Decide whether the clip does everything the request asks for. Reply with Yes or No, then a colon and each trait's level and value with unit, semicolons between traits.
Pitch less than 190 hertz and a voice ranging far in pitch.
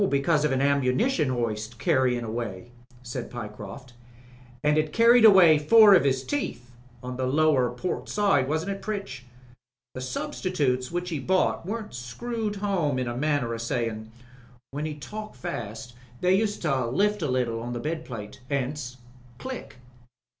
Yes: medium, 140 Hz; wide, 7.0 semitones